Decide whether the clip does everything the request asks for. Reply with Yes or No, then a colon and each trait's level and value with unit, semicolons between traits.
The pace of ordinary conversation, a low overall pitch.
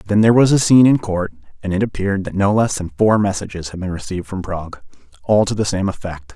No: fast, 245 wpm; low, 100 Hz